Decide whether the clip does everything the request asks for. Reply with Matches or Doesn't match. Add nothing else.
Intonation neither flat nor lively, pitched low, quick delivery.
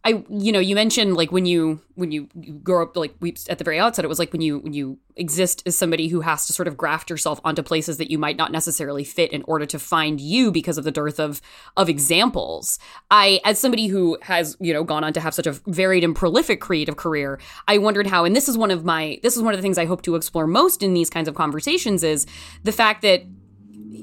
Doesn't match